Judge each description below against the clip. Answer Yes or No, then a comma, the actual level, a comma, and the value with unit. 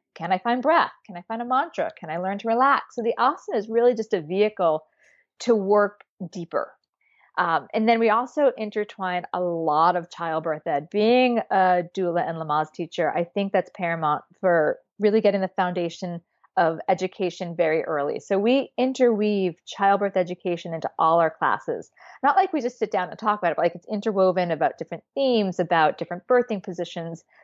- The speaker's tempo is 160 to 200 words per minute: Yes, average, 190 wpm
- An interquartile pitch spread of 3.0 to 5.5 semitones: Yes, average, 4.4 semitones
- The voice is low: No, high, 190 Hz